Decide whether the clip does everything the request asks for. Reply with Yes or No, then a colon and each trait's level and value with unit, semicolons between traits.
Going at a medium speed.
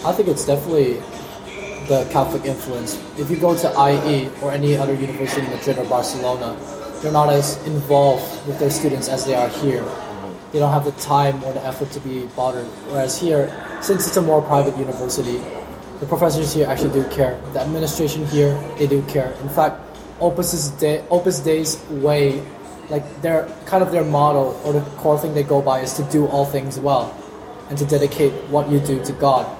Yes: average, 195 wpm